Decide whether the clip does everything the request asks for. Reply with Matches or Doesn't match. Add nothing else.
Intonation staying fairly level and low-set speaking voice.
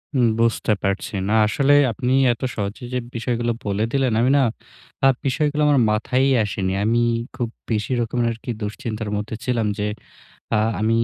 Doesn't match